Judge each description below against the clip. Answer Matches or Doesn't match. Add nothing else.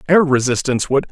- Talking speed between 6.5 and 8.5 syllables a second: Matches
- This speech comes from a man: Matches